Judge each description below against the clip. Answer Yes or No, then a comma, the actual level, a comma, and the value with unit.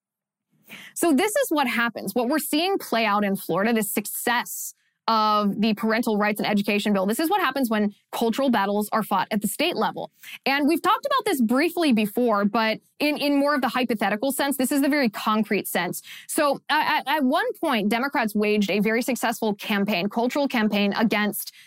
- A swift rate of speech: No, average, 190 wpm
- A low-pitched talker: No, high, 230 Hz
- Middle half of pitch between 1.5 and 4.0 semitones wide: No, average, 5.1 semitones